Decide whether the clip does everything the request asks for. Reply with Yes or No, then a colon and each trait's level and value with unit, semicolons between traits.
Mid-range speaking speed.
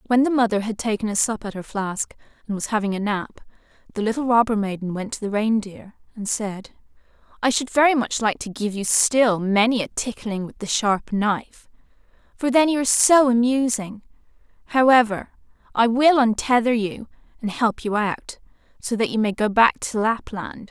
Yes: average, 185 wpm